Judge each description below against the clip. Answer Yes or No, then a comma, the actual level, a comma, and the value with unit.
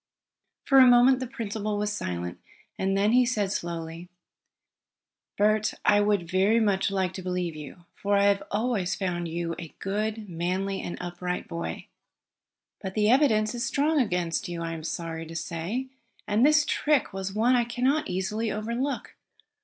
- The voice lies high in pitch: Yes, high, 200 Hz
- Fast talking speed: No, average, 165 wpm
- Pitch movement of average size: Yes, average, 4.7 semitones